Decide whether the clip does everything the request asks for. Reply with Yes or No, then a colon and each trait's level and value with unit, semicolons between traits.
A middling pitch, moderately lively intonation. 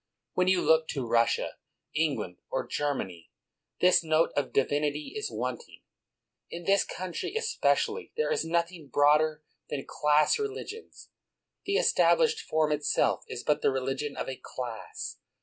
Yes: medium, 155 Hz; average, 4.7 semitones